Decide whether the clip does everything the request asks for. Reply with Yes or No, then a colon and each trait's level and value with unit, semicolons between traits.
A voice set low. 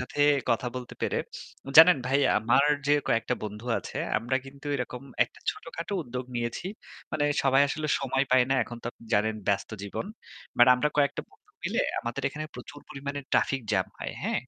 Yes: low, 130 Hz